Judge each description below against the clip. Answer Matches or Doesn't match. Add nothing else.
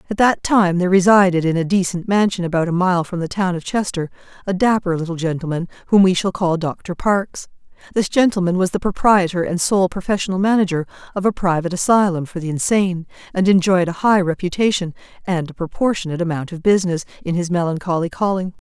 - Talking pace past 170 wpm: Matches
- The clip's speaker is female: Matches